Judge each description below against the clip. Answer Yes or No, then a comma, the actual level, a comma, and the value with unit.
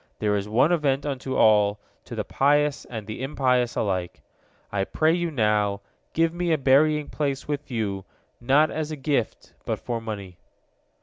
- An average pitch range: No, wide, 5.8 semitones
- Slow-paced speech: No, average, 170 wpm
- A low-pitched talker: Yes, low, 130 Hz